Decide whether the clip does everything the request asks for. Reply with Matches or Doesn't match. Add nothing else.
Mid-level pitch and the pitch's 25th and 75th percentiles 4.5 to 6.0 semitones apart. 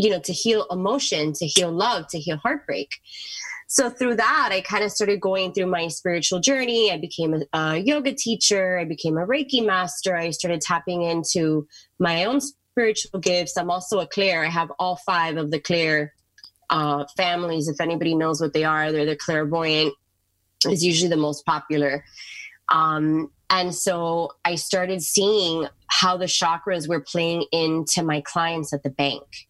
Doesn't match